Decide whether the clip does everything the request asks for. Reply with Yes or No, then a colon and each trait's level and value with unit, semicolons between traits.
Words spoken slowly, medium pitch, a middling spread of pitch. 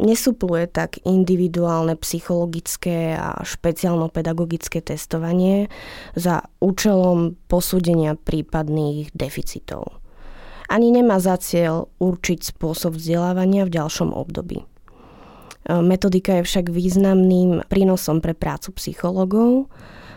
No: slow, 90 wpm; medium, 175 Hz; narrow, 2.1 semitones